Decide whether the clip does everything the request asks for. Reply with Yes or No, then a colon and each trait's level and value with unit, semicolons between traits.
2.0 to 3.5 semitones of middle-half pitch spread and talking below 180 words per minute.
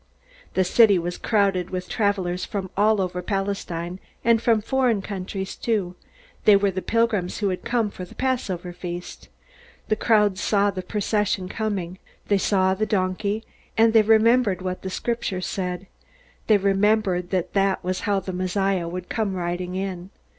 Yes: narrow, 2.6 semitones; average, 165 wpm